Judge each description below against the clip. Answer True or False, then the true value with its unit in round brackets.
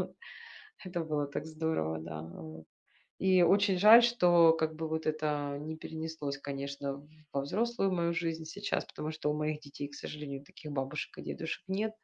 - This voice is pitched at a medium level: True (155 Hz)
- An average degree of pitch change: True (3.2 semitones)